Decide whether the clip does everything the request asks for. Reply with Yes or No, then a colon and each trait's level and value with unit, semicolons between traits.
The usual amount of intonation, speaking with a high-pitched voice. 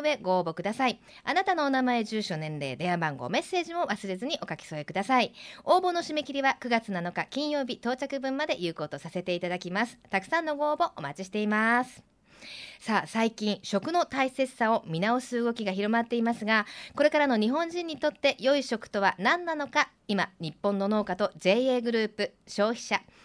No: wide, 6.2 semitones; high, 225 Hz